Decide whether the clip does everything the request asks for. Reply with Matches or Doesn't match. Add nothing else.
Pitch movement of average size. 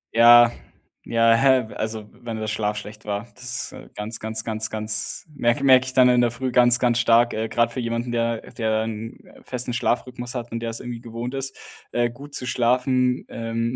Doesn't match